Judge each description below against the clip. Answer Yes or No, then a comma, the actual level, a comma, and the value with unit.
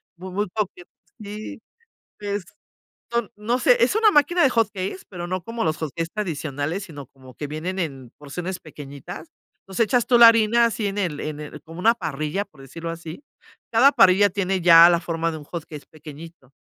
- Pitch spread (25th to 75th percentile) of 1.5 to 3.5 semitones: No, average, 5.2 semitones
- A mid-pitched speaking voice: Yes, medium, 180 Hz